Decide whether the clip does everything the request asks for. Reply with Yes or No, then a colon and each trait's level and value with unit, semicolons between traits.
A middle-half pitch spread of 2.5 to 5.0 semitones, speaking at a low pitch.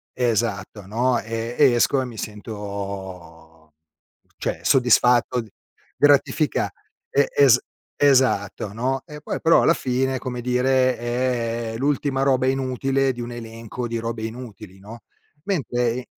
Yes: average, 2.8 semitones; low, 120 Hz